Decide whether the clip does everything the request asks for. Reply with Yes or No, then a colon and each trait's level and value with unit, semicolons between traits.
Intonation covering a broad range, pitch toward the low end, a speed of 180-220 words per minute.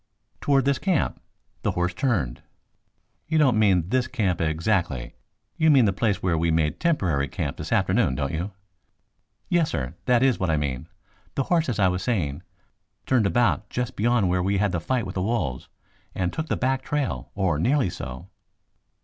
Yes: wide, 7.5 semitones; low, 100 Hz; average, 185 wpm